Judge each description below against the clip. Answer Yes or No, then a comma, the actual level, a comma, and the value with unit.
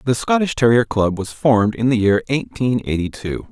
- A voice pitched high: No, low, 115 Hz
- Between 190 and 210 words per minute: Yes, fast, 205 wpm